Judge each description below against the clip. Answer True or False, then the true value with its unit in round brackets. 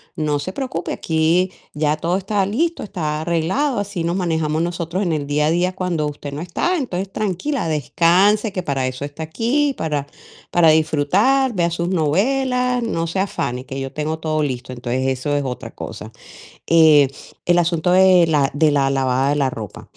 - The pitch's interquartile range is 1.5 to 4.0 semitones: False (4.4 semitones)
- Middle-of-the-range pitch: True (165 Hz)